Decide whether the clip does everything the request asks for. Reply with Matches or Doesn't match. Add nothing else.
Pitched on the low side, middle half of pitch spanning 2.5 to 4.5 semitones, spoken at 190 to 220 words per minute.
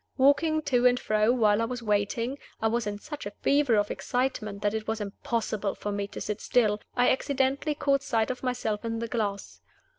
Doesn't match